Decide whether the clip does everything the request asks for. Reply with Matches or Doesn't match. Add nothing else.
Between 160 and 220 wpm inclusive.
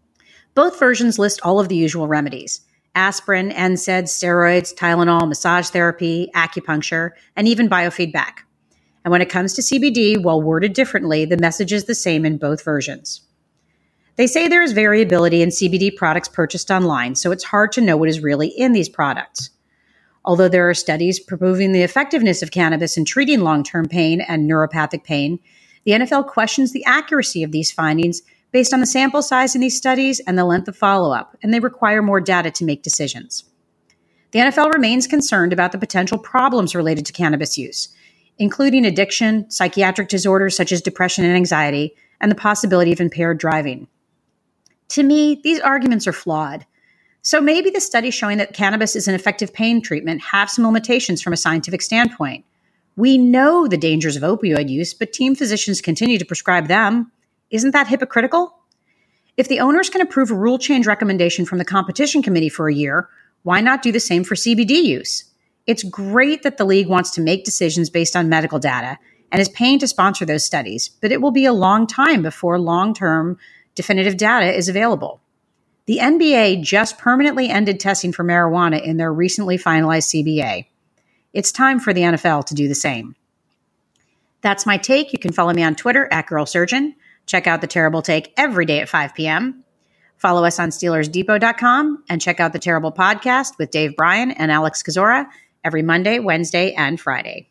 Matches